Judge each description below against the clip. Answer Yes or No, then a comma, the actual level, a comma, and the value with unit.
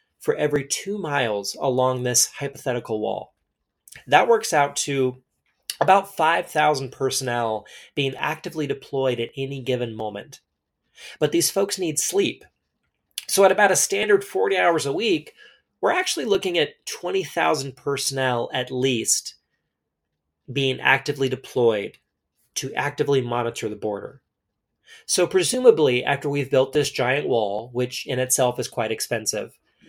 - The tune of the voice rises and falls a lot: Yes, wide, 6.0 semitones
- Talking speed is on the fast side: No, slow, 135 wpm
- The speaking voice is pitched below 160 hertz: Yes, medium, 140 Hz